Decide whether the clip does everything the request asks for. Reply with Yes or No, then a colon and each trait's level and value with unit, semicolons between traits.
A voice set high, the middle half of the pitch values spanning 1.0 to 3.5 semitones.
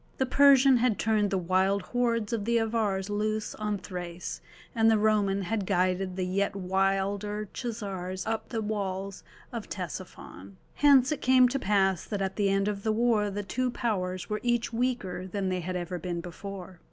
Yes: high, 205 Hz; average, 3.1 semitones